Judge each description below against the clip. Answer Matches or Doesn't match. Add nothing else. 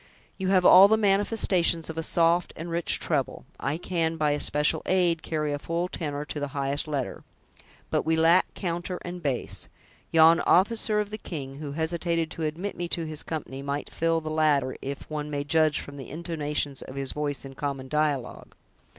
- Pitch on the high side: Doesn't match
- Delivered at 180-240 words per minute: Matches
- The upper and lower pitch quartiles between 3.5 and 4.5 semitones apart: Doesn't match